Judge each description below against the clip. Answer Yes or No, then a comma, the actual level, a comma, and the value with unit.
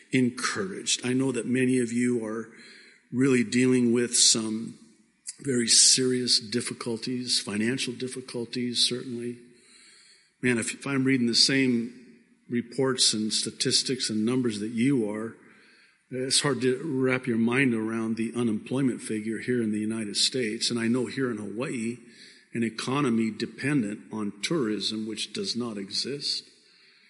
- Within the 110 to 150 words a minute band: Yes, average, 140 wpm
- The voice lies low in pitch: Yes, low, 120 Hz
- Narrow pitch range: Yes, narrow, 2.2 semitones